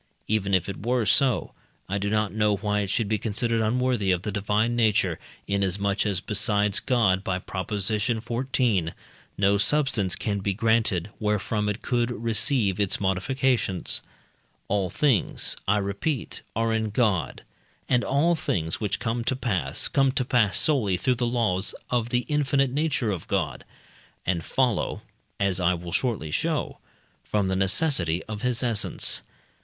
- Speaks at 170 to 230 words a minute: No, average, 155 wpm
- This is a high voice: No, low, 105 Hz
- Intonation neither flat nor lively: Yes, average, 3.8 semitones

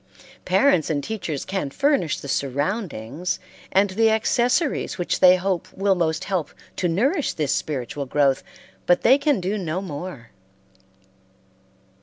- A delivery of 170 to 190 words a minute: No, slow, 135 wpm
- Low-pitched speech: No, medium, 180 Hz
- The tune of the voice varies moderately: No, wide, 6.1 semitones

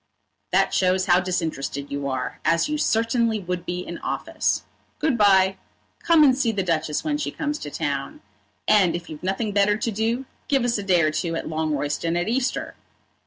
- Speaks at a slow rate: No, average, 190 wpm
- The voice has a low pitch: No, high, 190 Hz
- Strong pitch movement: Yes, wide, 5.9 semitones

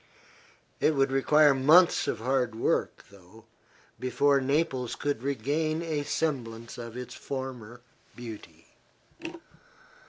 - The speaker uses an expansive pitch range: No, average, 3.8 semitones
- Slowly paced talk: Yes, slow, 105 wpm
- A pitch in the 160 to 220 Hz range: No, low, 135 Hz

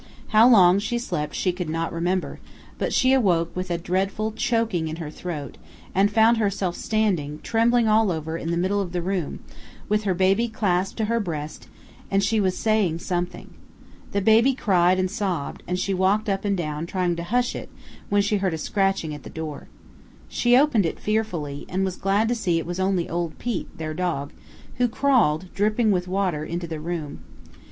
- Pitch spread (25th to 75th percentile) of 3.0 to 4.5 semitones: Yes, average, 4.0 semitones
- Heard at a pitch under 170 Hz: No, medium, 185 Hz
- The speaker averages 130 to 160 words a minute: No, average, 195 wpm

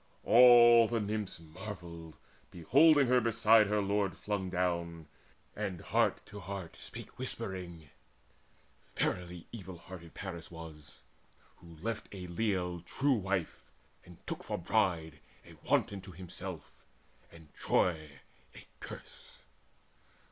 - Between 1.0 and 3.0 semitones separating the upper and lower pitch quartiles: No, average, 3.8 semitones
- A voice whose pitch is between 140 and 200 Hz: No, very low, 90 Hz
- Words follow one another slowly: Yes, slow, 120 wpm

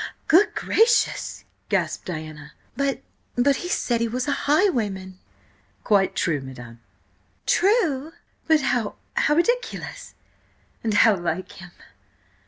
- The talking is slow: Yes, slow, 100 wpm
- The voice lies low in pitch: No, high, 240 Hz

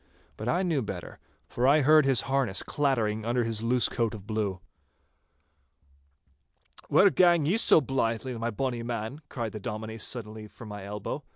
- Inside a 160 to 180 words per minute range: Yes, average, 165 wpm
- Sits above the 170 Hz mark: No, low, 115 Hz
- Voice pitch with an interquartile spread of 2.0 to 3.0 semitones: No, average, 3.9 semitones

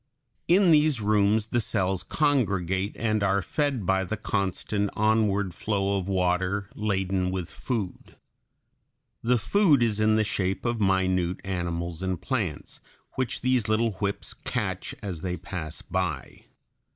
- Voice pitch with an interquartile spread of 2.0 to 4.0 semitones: Yes, average, 3.1 semitones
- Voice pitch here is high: No, low, 100 Hz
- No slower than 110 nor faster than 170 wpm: Yes, average, 140 wpm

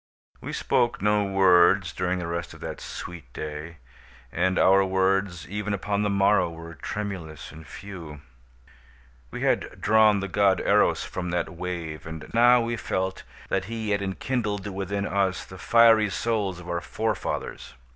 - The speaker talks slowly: No, average, 155 wpm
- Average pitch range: Yes, average, 3.0 semitones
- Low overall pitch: Yes, very low, 95 Hz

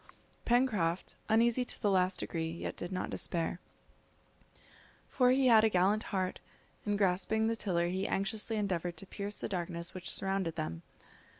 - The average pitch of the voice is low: No, high, 195 Hz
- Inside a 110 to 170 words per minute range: Yes, average, 160 wpm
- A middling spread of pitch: Yes, average, 3.8 semitones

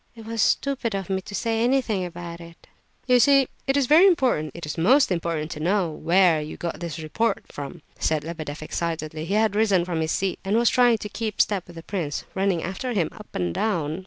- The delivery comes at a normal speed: No, fast, 220 wpm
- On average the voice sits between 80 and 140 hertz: No, medium, 185 Hz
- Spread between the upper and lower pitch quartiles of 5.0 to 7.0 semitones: Yes, wide, 5.4 semitones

